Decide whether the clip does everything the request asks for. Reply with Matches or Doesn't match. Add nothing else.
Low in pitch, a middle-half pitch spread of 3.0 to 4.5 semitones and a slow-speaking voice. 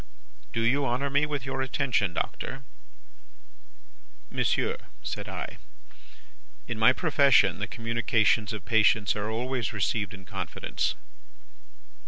Matches